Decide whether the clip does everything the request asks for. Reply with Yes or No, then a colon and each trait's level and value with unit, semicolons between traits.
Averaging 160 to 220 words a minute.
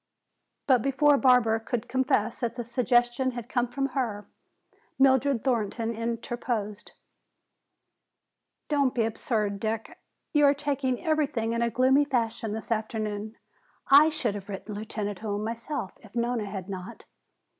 No: slow, 135 wpm